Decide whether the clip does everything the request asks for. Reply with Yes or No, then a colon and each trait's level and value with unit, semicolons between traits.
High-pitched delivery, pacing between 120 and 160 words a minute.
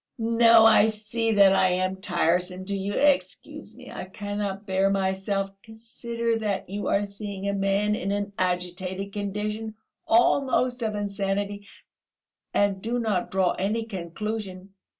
Yes: high, 200 Hz; average, 140 wpm